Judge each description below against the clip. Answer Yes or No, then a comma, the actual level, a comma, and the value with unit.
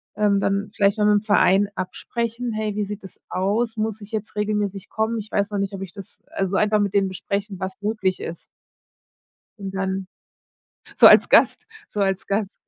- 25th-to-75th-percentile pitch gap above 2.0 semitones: No, narrow, 1.6 semitones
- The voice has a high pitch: Yes, high, 205 Hz